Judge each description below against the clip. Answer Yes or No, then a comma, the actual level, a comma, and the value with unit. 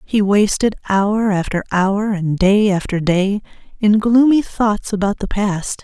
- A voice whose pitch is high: Yes, high, 205 Hz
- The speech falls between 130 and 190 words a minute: Yes, average, 155 wpm